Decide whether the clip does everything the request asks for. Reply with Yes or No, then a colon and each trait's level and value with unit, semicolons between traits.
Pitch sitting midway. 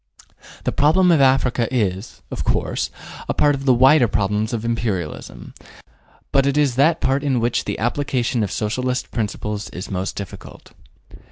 No: low, 120 Hz